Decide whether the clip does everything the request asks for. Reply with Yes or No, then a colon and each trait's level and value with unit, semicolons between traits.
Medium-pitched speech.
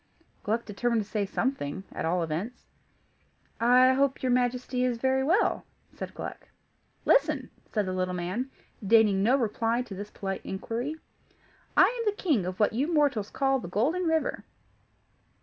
No: high, 235 Hz